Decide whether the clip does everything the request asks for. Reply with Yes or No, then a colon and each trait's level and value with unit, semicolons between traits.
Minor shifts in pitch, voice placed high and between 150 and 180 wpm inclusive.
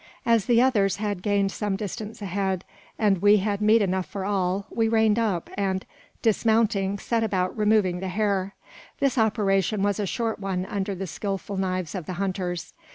Yes: narrow, 2.2 semitones; high, 200 Hz; average, 175 wpm